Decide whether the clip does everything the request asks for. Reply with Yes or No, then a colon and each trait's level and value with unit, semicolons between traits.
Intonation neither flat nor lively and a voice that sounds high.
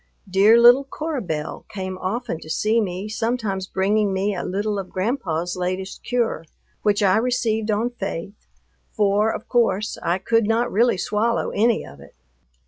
Yes: average, 3.5 semitones; high, 210 Hz